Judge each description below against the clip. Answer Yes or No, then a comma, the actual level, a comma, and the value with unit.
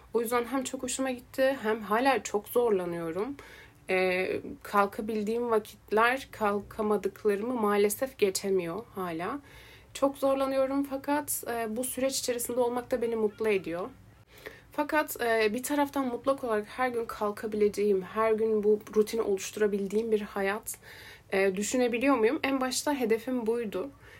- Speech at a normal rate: Yes, average, 130 wpm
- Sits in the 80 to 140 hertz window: No, high, 225 Hz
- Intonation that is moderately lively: Yes, average, 3.8 semitones